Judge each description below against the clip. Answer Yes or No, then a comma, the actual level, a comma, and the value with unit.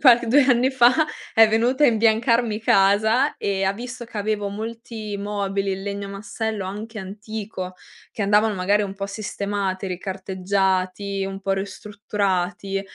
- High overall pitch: Yes, high, 205 Hz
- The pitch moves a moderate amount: No, narrow, 2.2 semitones